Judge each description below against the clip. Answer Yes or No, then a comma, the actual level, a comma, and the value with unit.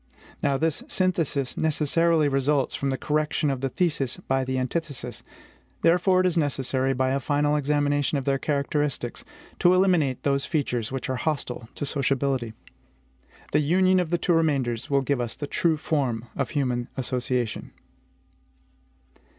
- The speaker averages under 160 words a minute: Yes, average, 150 wpm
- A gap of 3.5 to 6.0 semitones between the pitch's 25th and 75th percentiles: No, average, 3.0 semitones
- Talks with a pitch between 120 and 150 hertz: Yes, medium, 140 Hz